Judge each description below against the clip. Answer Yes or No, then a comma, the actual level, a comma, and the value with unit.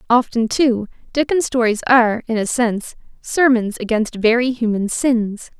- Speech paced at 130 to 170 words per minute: Yes, average, 140 wpm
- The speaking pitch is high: Yes, high, 235 Hz